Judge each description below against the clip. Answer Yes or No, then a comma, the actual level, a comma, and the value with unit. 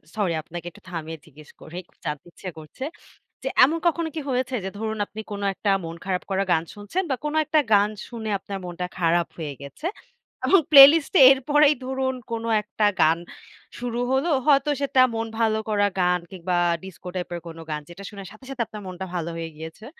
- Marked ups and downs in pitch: Yes, wide, 7.1 semitones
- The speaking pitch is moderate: No, high, 205 Hz